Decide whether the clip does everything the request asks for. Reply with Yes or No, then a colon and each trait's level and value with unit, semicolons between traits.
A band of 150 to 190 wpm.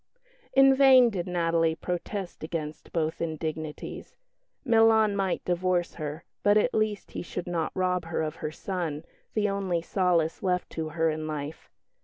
Yes: average, 155 wpm